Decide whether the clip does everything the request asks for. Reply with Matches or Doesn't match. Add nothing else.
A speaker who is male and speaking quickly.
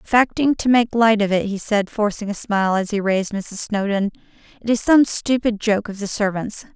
Doesn't match